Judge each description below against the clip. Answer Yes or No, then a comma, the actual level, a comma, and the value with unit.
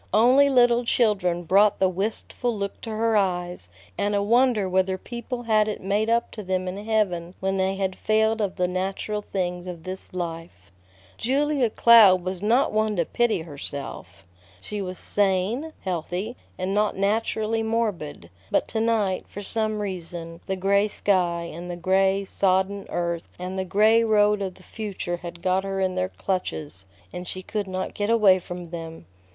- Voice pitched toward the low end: No, high, 195 Hz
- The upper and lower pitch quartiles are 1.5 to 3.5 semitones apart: Yes, average, 3.1 semitones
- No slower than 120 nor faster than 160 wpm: No, average, 175 wpm